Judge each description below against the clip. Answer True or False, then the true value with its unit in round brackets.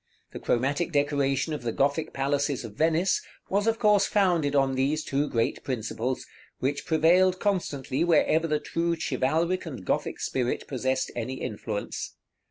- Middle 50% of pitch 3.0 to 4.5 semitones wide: True (4.1 semitones)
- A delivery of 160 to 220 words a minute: False (150 wpm)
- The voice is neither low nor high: True (145 Hz)